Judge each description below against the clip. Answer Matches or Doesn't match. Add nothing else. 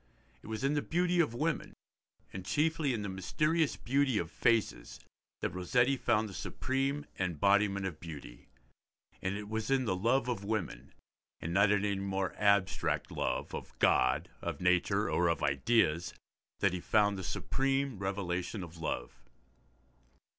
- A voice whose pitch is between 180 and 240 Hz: Doesn't match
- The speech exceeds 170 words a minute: Doesn't match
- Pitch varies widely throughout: Matches